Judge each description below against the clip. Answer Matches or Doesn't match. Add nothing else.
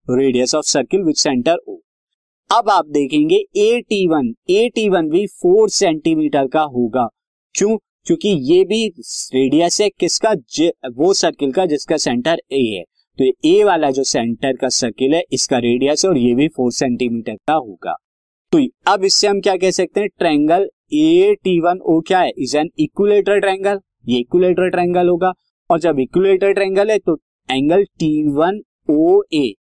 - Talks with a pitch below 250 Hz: Matches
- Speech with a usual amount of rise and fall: Doesn't match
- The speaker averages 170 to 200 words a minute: Matches